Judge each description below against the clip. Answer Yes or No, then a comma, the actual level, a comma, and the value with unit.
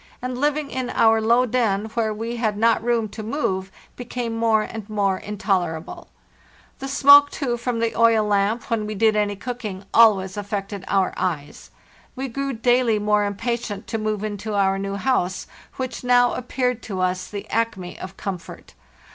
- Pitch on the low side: No, high, 220 Hz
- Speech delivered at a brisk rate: No, average, 170 wpm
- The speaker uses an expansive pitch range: No, average, 3.3 semitones